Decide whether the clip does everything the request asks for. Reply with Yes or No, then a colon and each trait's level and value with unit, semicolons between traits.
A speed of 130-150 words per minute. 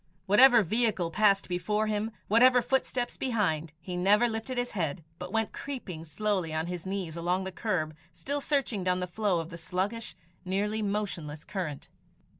No: average, 165 wpm